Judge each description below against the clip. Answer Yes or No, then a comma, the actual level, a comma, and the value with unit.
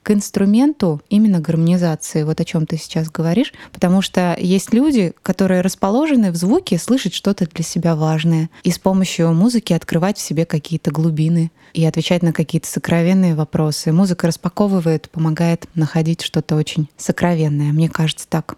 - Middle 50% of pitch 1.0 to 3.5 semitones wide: Yes, average, 2.9 semitones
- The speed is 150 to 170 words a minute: Yes, average, 155 wpm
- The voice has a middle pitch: Yes, medium, 170 Hz